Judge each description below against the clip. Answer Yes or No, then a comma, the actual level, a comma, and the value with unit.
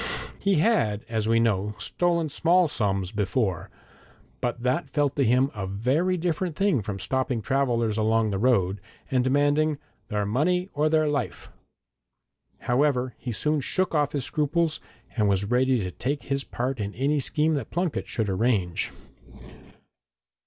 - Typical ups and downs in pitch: No, wide, 5.7 semitones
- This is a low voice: Yes, low, 130 Hz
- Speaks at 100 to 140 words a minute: No, average, 150 wpm